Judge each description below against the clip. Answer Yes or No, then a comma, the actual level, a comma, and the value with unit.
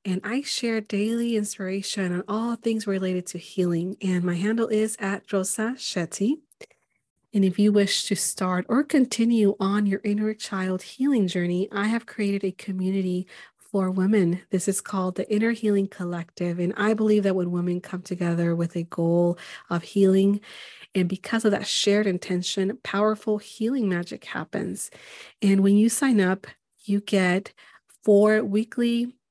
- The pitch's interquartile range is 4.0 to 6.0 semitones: No, average, 2.8 semitones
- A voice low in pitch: No, high, 200 Hz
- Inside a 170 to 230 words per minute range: No, average, 160 wpm